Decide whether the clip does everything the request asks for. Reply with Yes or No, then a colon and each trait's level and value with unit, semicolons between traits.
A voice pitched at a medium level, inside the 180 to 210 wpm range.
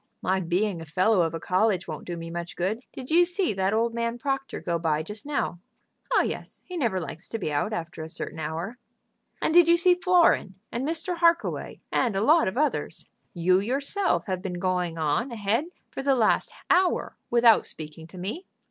No: high, 210 Hz; average, 200 wpm